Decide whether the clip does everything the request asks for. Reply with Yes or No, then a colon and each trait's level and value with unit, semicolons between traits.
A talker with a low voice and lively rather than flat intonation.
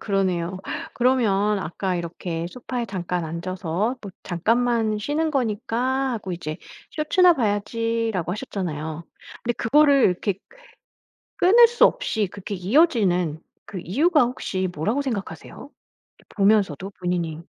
No: high, 205 Hz; wide, 5.8 semitones